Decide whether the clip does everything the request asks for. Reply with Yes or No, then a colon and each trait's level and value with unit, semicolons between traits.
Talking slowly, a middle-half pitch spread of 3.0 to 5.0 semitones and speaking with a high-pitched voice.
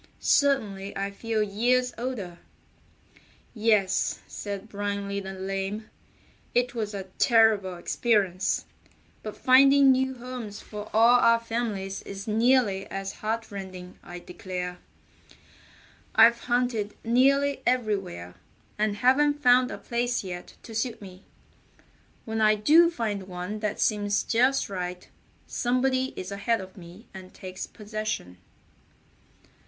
Yes: slow, 120 wpm; average, 3.9 semitones; high, 215 Hz